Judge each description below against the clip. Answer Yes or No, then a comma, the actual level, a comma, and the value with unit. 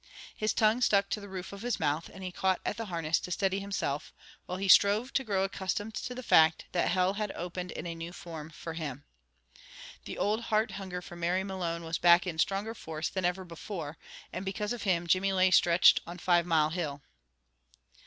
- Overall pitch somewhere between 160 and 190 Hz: Yes, medium, 185 Hz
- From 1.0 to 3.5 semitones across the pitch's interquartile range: Yes, average, 2.9 semitones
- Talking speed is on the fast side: Yes, fast, 210 wpm